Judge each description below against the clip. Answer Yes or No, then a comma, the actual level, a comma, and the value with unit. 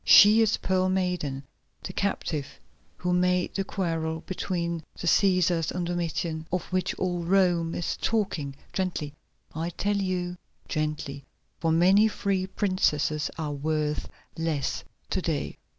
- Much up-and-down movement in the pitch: No, average, 2.9 semitones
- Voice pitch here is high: No, medium, 175 Hz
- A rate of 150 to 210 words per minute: No, slow, 135 wpm